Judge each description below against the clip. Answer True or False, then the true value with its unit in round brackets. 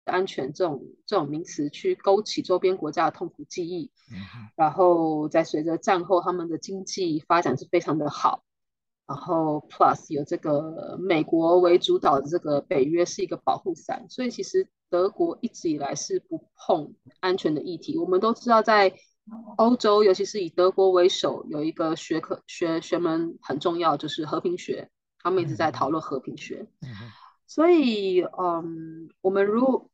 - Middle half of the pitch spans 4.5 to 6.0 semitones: True (5.6 semitones)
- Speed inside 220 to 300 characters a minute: True (260 characters per minute)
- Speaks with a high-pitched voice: False (180 Hz)